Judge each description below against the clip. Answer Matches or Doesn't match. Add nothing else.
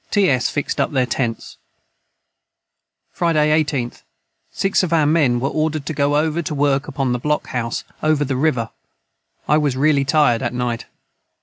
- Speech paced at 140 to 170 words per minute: Matches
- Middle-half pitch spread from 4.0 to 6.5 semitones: Doesn't match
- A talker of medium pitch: Matches